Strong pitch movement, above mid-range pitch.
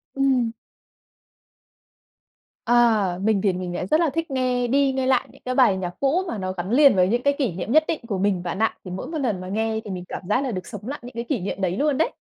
Yes: wide, 6.0 semitones; high, 230 Hz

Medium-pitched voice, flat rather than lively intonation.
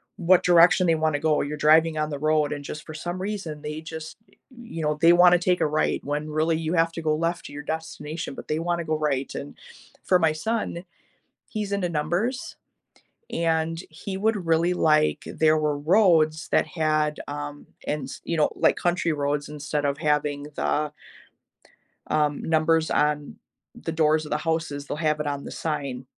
Yes: medium, 155 Hz; narrow, 2.0 semitones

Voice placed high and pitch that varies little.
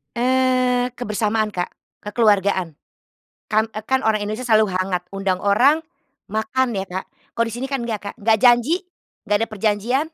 No: high, 220 Hz; average, 3.4 semitones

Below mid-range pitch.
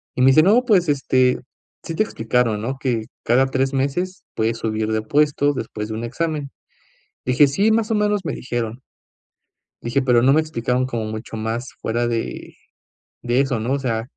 Yes: low, 130 Hz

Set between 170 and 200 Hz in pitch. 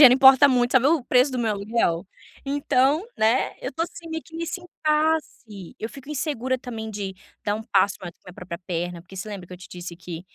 No: high, 240 Hz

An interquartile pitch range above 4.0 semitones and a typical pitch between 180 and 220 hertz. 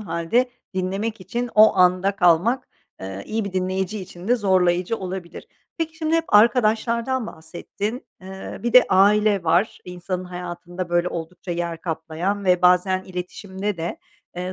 No: average, 3.3 semitones; medium, 185 Hz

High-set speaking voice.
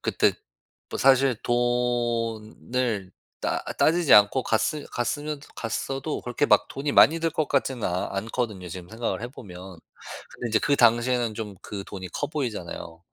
No: low, 120 Hz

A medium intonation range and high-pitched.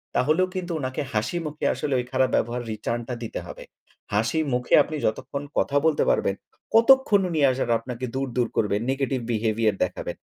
No: average, 4.9 semitones; low, 130 Hz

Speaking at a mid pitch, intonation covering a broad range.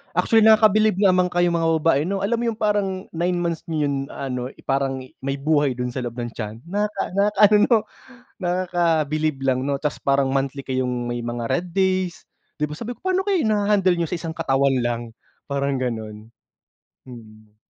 Yes: medium, 155 Hz; wide, 6.5 semitones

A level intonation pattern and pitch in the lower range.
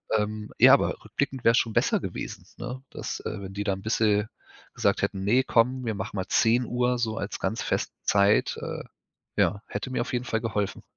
No: average, 3.1 semitones; low, 110 Hz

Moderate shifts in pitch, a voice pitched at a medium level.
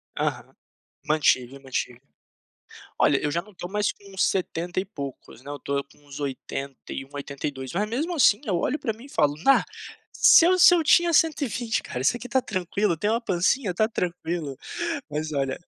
No: wide, 8.0 semitones; medium, 175 Hz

